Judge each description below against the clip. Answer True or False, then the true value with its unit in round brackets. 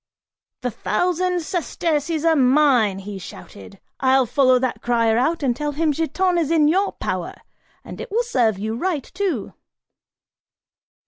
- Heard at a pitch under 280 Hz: False (290 Hz)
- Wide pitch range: True (6.0 semitones)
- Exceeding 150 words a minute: False (145 wpm)